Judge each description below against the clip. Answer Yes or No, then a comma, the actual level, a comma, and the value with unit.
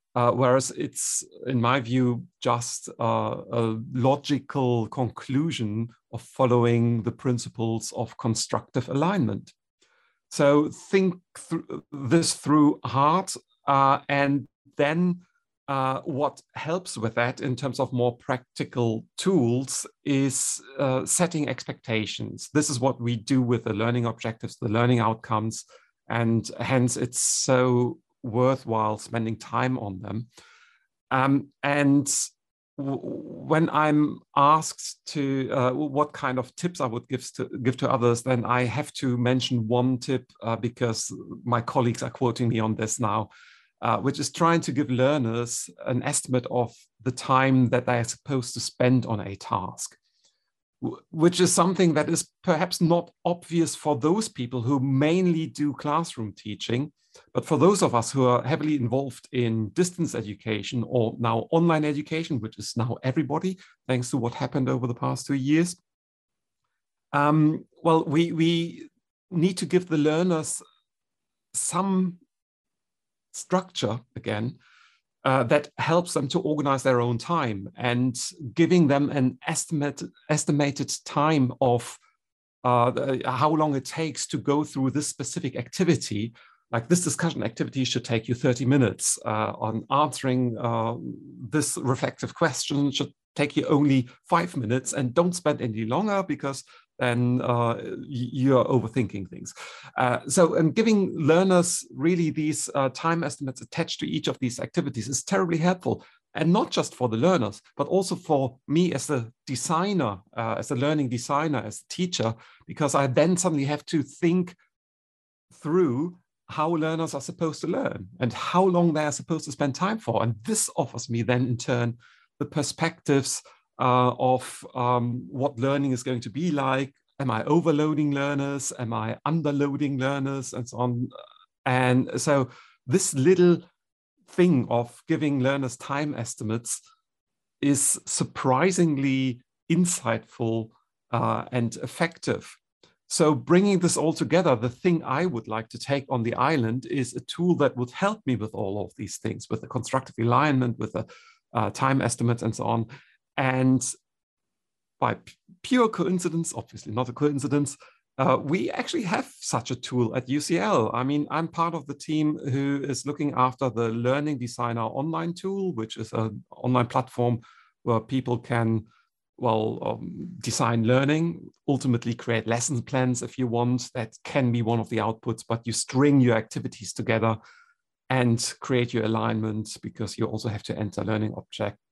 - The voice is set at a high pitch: No, low, 135 Hz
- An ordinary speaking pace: Yes, average, 155 wpm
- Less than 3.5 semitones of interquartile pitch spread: No, average, 4.3 semitones